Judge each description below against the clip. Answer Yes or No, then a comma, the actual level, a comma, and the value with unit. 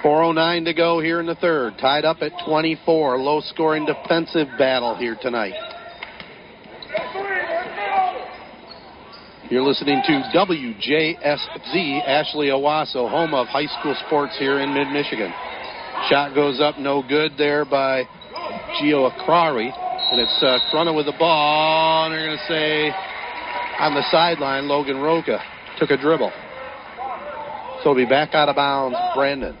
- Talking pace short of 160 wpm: Yes, average, 140 wpm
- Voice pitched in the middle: Yes, medium, 155 Hz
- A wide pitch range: No, average, 2.7 semitones